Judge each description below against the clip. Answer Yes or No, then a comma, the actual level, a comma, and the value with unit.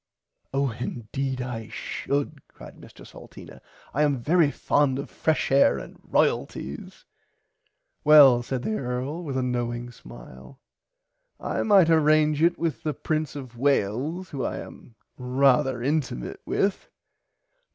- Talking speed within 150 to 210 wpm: No, average, 140 wpm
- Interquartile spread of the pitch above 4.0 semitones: No, average, 3.7 semitones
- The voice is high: No, low, 135 Hz